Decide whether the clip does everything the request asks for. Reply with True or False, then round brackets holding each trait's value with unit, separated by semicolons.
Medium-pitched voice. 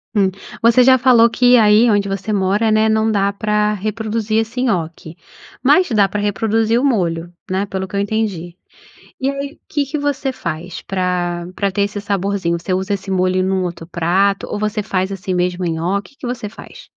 False (200 Hz)